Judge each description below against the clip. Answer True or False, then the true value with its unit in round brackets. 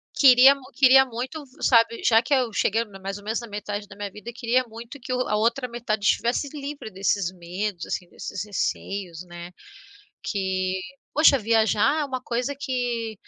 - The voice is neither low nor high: False (230 Hz)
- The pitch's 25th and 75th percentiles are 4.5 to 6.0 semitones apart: False (4.0 semitones)